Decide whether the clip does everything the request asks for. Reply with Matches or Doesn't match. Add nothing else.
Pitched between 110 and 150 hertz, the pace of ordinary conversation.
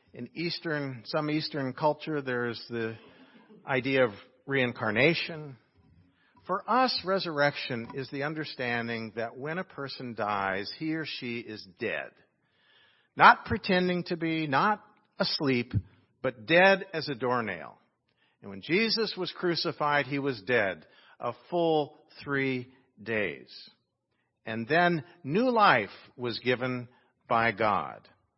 Doesn't match